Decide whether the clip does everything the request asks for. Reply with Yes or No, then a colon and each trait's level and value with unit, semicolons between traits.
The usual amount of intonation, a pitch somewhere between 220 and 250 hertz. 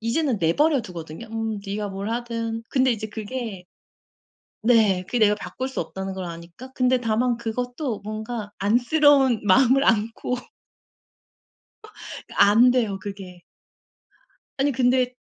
Yes: average, 3.6 semitones; high, 225 Hz